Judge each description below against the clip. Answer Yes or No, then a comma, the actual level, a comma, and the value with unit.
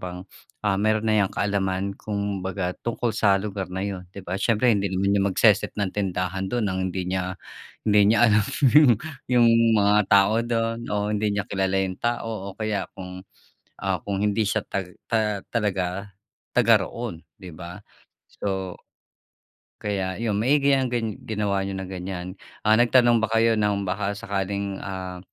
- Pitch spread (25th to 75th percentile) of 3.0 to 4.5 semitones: No, narrow, 2.4 semitones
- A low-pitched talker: Yes, low, 100 Hz